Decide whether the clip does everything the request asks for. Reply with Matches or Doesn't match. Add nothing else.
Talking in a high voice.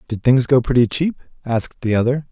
Doesn't match